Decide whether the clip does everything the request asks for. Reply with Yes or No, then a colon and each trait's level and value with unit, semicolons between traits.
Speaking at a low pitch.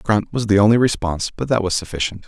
Yes: low, 105 Hz